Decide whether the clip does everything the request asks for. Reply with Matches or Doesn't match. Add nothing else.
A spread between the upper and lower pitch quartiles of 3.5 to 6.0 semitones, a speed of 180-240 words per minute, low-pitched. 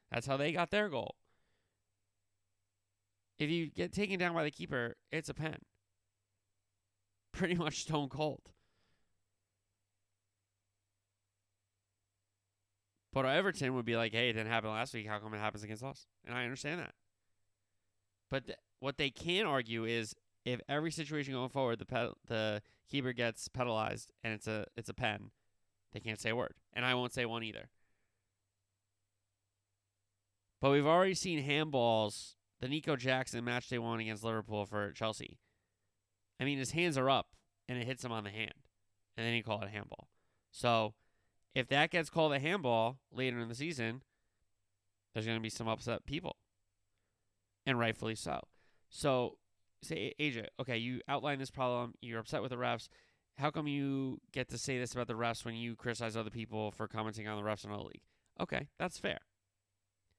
Doesn't match